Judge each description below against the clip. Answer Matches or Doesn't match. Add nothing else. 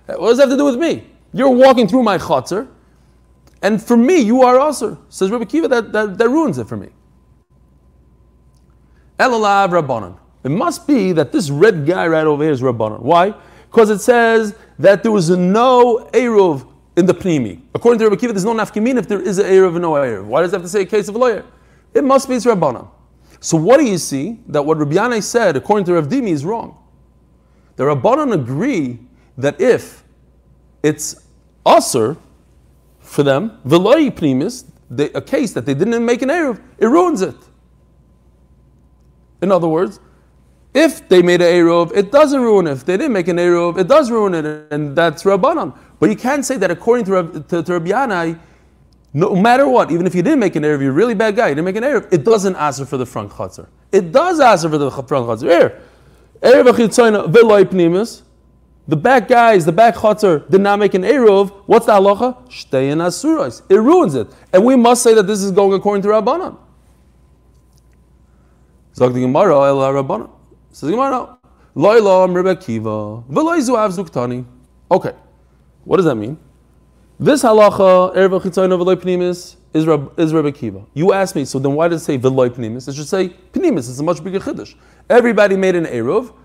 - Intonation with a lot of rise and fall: Matches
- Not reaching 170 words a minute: Doesn't match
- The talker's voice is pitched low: Doesn't match